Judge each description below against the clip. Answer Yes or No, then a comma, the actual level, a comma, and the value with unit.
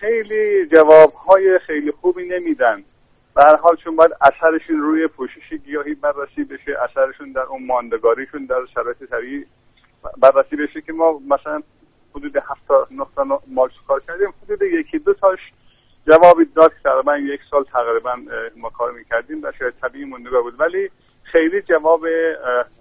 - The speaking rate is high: No, average, 145 wpm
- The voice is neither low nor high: Yes, medium, 160 Hz